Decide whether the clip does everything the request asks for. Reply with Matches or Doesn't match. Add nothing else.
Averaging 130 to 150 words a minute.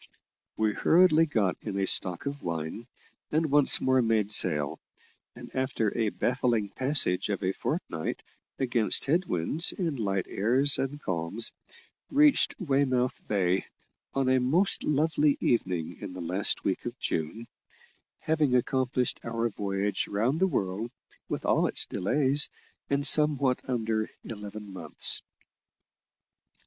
Matches